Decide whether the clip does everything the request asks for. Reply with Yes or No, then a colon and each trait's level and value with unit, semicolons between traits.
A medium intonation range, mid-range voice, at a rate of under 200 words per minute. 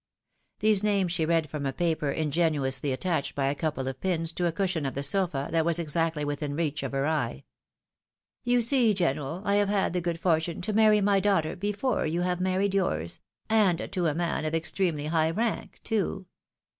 No: average, 4.4 semitones; medium, 170 Hz; fast, 205 wpm